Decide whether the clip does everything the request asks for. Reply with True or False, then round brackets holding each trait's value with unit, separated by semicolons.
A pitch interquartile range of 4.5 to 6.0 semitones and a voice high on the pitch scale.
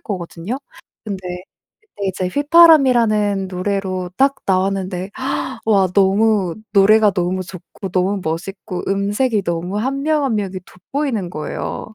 False (3.2 semitones; 195 Hz)